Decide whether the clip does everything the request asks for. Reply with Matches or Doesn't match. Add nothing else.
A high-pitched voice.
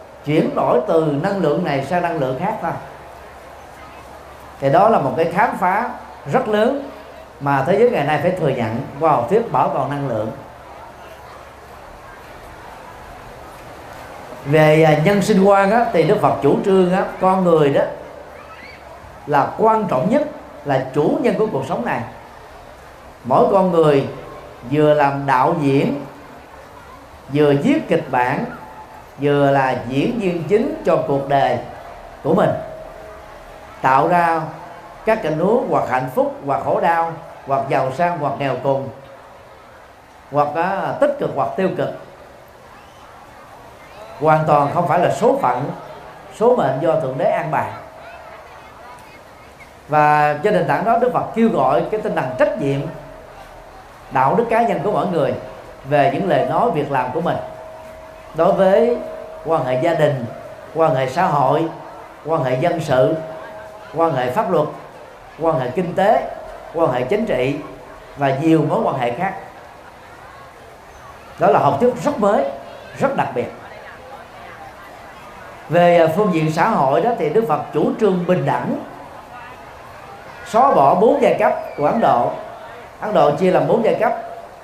Doesn't match